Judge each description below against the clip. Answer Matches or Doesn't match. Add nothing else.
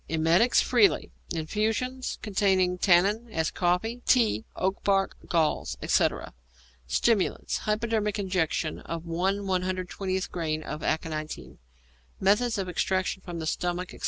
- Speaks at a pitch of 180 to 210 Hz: Matches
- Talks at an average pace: Doesn't match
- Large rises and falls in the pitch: Doesn't match